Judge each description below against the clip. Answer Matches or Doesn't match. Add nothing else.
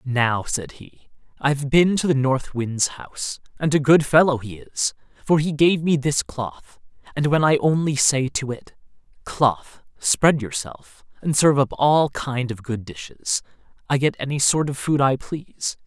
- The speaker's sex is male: Matches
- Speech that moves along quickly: Doesn't match